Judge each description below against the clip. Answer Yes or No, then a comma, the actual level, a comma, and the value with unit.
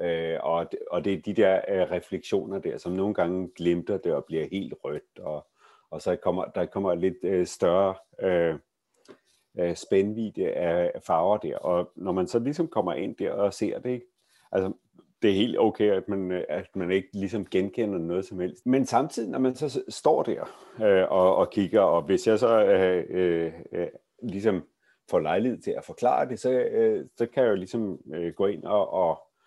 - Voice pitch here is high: No, very low, 95 Hz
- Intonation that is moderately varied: No, wide, 5.8 semitones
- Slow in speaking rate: No, average, 195 wpm